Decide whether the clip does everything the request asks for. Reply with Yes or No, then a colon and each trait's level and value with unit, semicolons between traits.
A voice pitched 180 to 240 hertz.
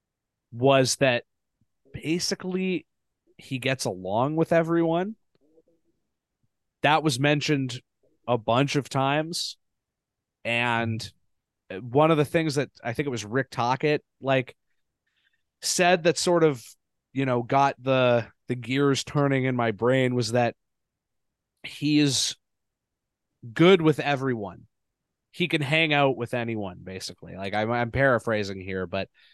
No: low, 135 Hz